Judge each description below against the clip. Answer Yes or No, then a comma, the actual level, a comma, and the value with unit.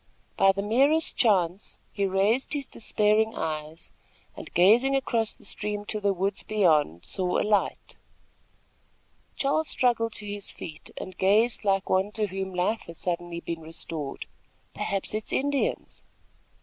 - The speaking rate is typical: Yes, average, 150 wpm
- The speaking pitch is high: Yes, high, 200 Hz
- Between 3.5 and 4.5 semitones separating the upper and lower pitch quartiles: Yes, average, 3.8 semitones